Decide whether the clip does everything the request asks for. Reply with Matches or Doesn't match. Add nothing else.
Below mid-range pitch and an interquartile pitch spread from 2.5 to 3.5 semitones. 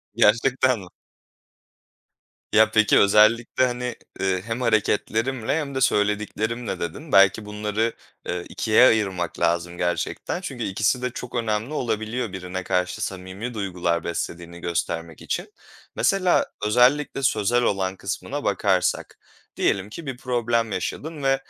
Doesn't match